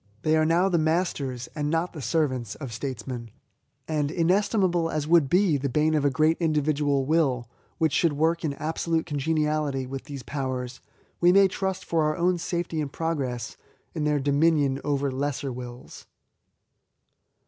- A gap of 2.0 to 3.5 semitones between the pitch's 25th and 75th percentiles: Yes, average, 3.2 semitones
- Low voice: No, medium, 150 Hz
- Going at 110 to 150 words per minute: No, average, 160 wpm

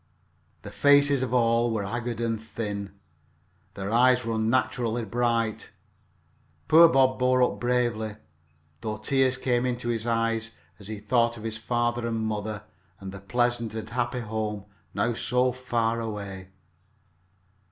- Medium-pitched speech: No, low, 115 Hz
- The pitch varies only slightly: Yes, narrow, 2.0 semitones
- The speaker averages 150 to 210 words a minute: No, average, 140 wpm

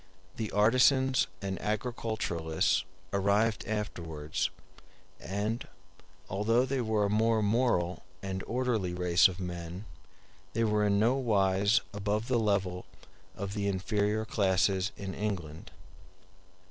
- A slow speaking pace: Yes, slow, 110 wpm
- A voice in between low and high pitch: No, low, 105 Hz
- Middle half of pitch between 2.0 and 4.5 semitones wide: Yes, average, 2.9 semitones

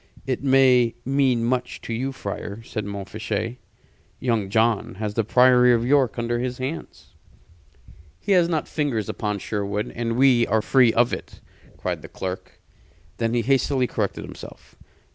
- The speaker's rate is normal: Yes, average, 155 wpm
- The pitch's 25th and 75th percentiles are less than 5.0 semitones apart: Yes, average, 3.0 semitones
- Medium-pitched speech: No, low, 120 Hz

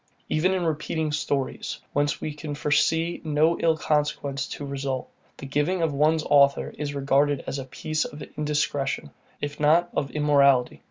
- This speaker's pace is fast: No, average, 160 wpm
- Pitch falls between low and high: Yes, medium, 150 Hz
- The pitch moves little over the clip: Yes, narrow, 1.9 semitones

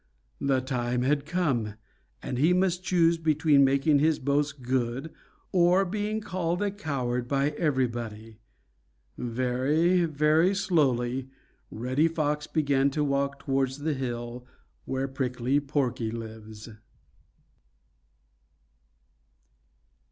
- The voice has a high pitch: No, medium, 140 Hz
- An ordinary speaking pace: No, slow, 105 wpm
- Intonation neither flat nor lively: Yes, average, 4.3 semitones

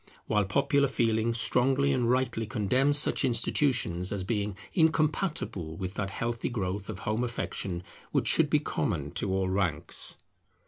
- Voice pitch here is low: Yes, low, 115 Hz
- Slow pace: No, average, 145 wpm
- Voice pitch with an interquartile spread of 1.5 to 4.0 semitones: No, average, 5.2 semitones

